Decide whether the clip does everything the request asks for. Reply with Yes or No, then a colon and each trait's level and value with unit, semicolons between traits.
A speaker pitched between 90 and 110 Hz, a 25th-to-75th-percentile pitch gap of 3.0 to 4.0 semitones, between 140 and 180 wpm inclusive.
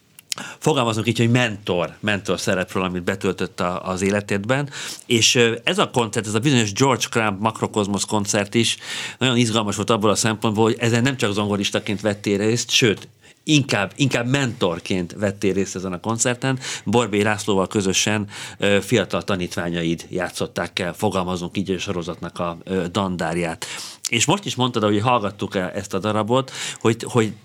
Yes: low, 105 Hz; average, 3.4 semitones; average, 150 wpm